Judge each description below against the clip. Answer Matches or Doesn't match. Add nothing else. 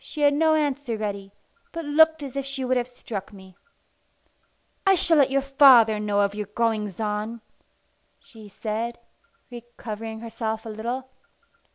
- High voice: Matches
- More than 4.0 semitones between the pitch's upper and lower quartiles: Matches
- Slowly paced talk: Doesn't match